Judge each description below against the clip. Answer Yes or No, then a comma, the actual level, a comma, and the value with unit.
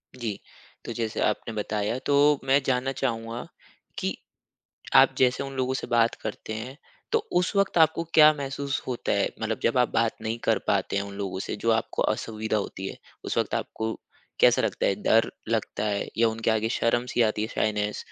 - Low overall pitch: Yes, low, 115 Hz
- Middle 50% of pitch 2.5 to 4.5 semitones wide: Yes, average, 3.6 semitones